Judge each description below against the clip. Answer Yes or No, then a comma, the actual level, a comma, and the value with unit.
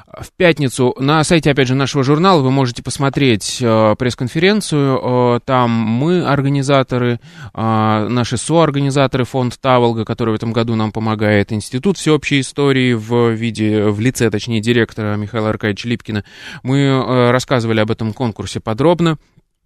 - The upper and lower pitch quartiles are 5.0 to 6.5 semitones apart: No, average, 3.7 semitones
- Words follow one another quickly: No, average, 130 wpm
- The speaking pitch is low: Yes, low, 125 Hz